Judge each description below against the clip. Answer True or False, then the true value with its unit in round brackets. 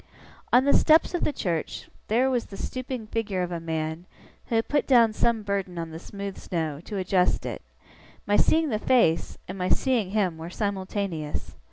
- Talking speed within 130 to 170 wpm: False (190 wpm)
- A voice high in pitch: True (200 Hz)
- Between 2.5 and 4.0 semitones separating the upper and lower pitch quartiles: False (5.2 semitones)